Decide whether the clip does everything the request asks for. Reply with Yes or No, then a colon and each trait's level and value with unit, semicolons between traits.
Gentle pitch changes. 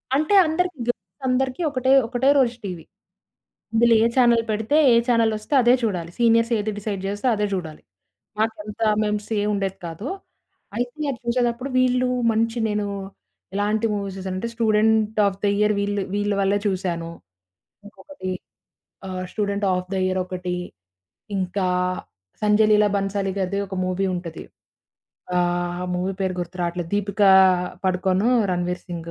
No: average, 3.7 semitones